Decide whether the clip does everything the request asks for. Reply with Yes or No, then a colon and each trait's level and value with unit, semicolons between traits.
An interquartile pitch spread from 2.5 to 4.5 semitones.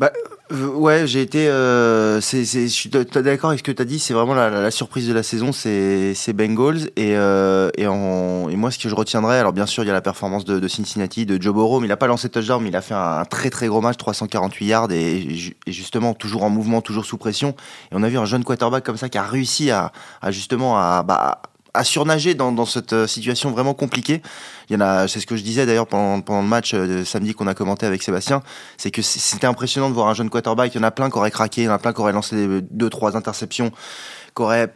Yes: average, 3.7 semitones